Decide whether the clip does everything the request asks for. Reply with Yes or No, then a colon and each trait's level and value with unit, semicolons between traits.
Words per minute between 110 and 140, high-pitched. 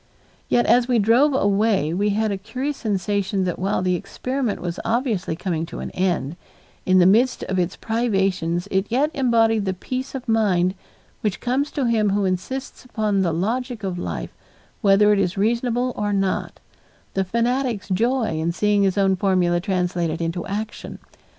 No: average, 170 wpm; high, 205 Hz